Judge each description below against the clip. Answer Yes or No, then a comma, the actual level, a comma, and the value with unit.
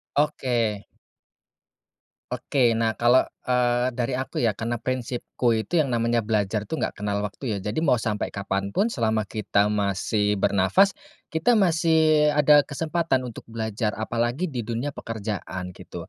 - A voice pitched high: No, low, 115 Hz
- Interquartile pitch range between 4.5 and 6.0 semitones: Yes, average, 4.8 semitones